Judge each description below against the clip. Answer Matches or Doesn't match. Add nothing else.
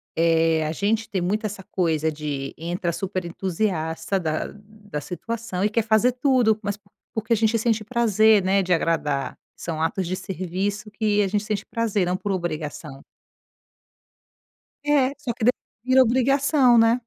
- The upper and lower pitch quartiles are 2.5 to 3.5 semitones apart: Doesn't match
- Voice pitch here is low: Doesn't match